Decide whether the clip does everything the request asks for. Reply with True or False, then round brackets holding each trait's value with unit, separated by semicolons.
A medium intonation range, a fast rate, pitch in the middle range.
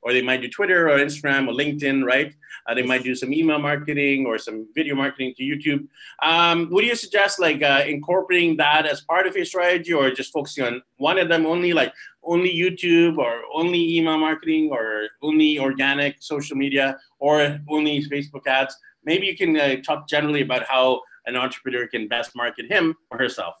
False (3.9 semitones; 195 wpm; 145 Hz)